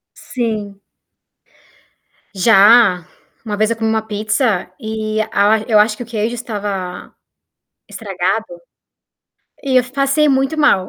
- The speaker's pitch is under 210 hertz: No, high, 220 Hz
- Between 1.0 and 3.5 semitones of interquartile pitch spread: Yes, average, 2.9 semitones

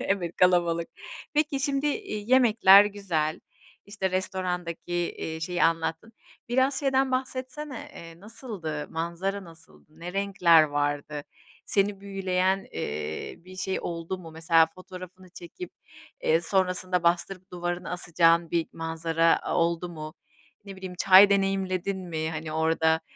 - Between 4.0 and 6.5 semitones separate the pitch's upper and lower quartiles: No, average, 3.1 semitones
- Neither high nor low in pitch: Yes, medium, 180 Hz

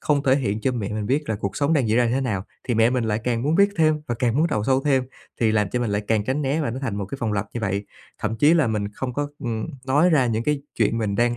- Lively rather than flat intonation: No, average, 4.3 semitones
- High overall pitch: No, low, 120 Hz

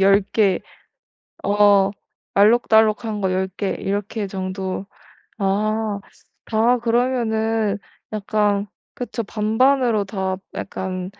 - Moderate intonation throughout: No, narrow, 2.1 semitones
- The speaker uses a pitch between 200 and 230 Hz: Yes, high, 210 Hz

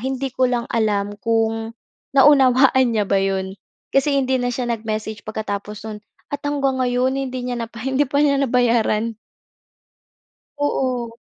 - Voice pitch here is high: Yes, high, 245 Hz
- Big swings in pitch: No, average, 3.4 semitones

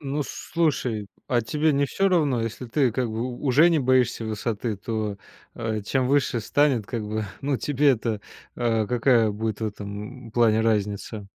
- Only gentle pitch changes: No, average, 3.9 semitones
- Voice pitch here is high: No, low, 120 Hz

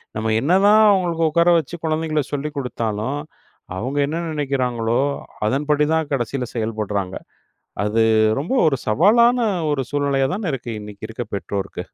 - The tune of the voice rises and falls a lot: Yes, wide, 6.0 semitones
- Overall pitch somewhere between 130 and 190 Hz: Yes, medium, 140 Hz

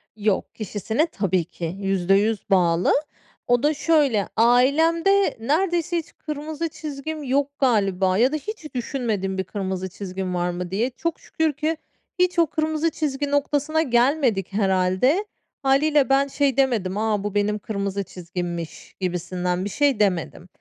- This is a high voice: Yes, high, 235 Hz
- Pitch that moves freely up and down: Yes, wide, 7.8 semitones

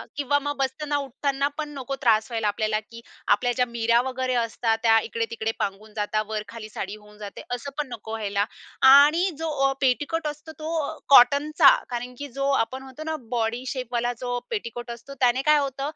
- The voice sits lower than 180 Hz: No, high, 245 Hz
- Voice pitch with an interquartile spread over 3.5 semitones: Yes, average, 4.0 semitones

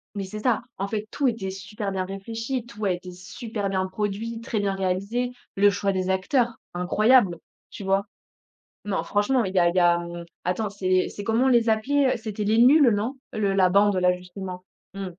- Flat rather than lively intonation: No, average, 3.2 semitones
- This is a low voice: No, high, 200 Hz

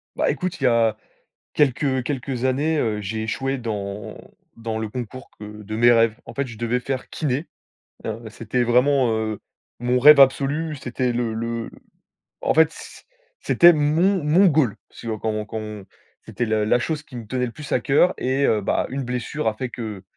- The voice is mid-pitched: No, low, 125 Hz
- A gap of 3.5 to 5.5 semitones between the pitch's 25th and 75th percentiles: Yes, average, 3.9 semitones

